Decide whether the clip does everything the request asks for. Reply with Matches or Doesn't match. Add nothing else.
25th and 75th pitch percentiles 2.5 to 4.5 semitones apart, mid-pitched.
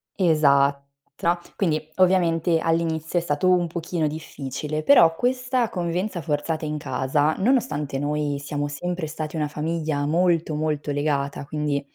Matches